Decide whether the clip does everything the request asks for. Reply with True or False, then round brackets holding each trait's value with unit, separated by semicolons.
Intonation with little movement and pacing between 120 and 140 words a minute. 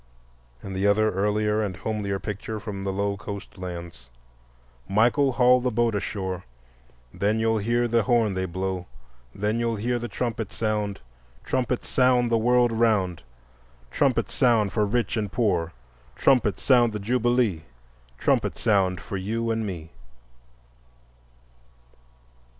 False (3.3 semitones; 135 wpm)